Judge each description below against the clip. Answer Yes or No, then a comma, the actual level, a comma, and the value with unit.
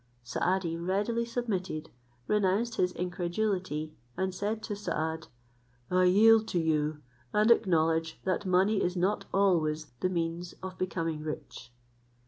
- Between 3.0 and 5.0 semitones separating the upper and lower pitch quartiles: Yes, average, 3.7 semitones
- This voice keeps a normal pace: No, slow, 125 wpm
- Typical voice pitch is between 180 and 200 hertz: Yes, medium, 185 Hz